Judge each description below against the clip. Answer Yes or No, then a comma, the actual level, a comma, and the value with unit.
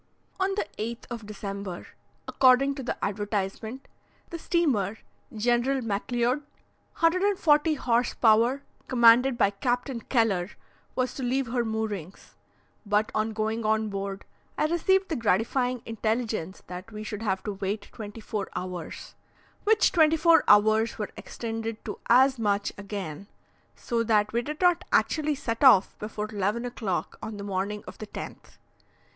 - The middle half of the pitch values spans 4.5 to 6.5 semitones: No, average, 3.8 semitones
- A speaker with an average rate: Yes, average, 145 wpm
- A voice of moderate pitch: No, high, 225 Hz